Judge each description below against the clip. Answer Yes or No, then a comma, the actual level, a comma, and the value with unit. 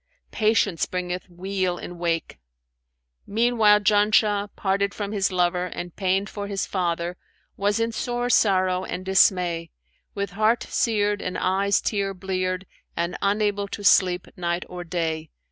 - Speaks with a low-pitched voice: No, high, 190 Hz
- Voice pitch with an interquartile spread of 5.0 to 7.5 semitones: No, narrow, 2.4 semitones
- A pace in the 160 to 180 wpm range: No, average, 140 wpm